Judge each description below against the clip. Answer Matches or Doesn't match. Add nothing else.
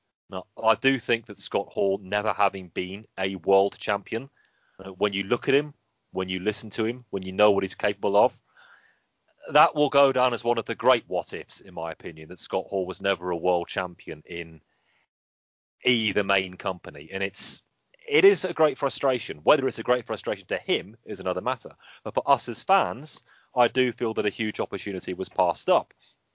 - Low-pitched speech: Matches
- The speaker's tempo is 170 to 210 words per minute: Matches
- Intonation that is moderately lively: Matches